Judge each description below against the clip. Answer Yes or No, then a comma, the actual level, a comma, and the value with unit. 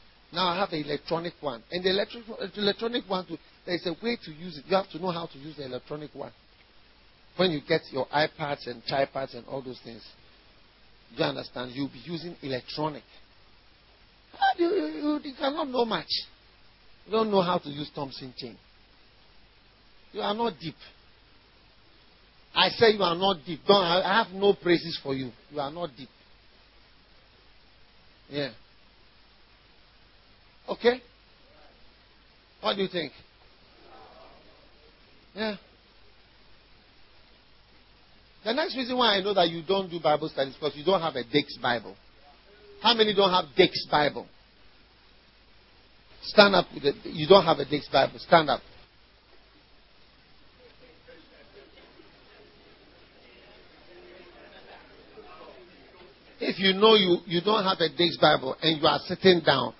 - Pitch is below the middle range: No, medium, 145 Hz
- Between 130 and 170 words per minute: Yes, average, 140 wpm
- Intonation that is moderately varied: No, wide, 8.9 semitones